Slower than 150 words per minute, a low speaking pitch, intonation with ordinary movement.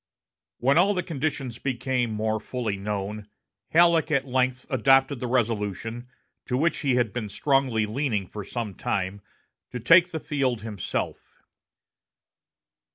Yes: slow, 135 wpm; low, 125 Hz; average, 4.3 semitones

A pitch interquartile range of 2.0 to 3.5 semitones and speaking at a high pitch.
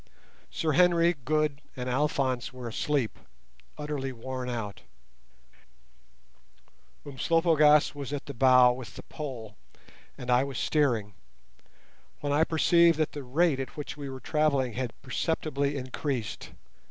No: average, 3.1 semitones; medium, 140 Hz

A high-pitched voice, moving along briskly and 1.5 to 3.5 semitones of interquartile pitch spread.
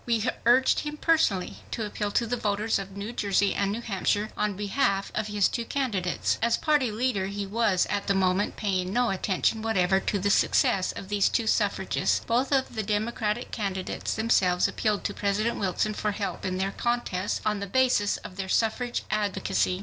No: high, 210 Hz; average, 190 wpm; average, 2.9 semitones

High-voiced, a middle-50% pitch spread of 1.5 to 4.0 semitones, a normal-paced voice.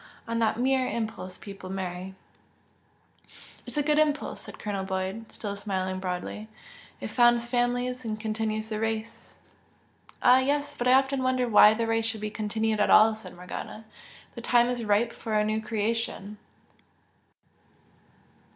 Yes: high, 220 Hz; average, 2.7 semitones; average, 150 wpm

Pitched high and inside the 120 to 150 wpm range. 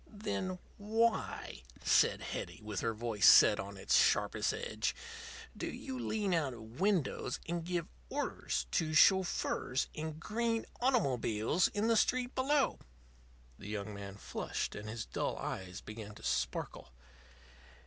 No: medium, 150 Hz; average, 140 wpm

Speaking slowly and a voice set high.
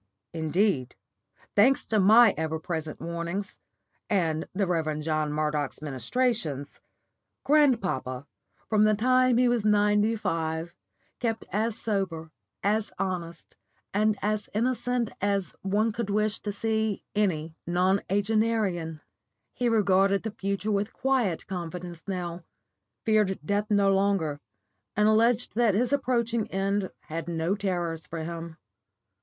Yes: slow, 125 wpm; high, 200 Hz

